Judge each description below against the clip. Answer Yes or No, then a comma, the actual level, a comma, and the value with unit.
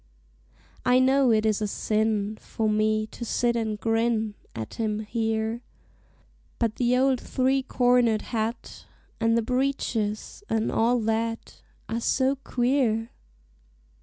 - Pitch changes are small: Yes, narrow, 2.3 semitones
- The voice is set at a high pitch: Yes, high, 225 Hz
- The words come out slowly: Yes, slow, 130 wpm